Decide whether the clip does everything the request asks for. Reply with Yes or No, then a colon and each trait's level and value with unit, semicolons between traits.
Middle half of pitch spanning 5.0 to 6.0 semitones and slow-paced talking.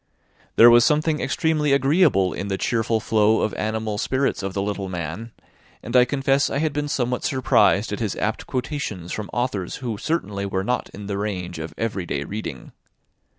No: wide, 5.4 semitones; average, 185 wpm